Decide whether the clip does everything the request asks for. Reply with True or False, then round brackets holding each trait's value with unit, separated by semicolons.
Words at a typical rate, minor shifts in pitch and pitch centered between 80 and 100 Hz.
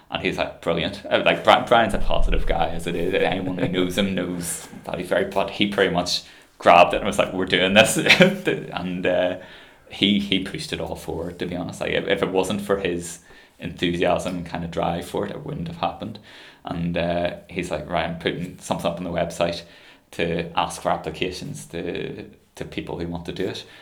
False (215 wpm; 1.6 semitones; 90 Hz)